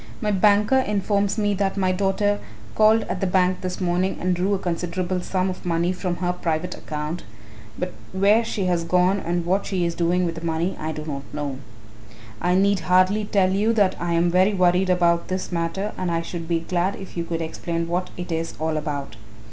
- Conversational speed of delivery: No, fast, 210 wpm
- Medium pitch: Yes, medium, 180 Hz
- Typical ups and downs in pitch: No, narrow, 2.3 semitones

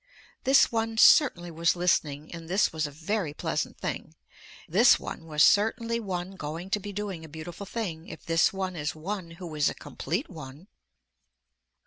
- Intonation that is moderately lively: Yes, average, 4.3 semitones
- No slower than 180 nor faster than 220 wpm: No, average, 170 wpm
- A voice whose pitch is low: No, medium, 175 Hz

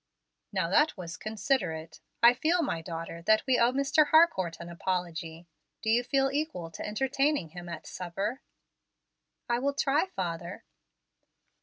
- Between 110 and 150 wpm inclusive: Yes, average, 145 wpm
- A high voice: Yes, high, 215 Hz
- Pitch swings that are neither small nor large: No, wide, 8.2 semitones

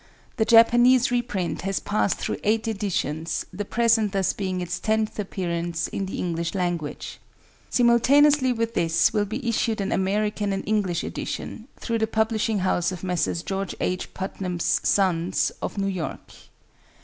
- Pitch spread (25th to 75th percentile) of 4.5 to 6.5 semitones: No, average, 3.7 semitones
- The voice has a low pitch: No, high, 200 Hz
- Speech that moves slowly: No, average, 150 wpm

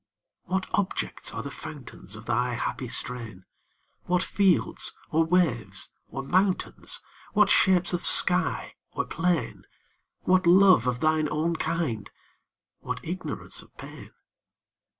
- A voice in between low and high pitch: Yes, medium, 160 Hz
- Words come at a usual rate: No, slow, 125 wpm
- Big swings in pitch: Yes, wide, 6.7 semitones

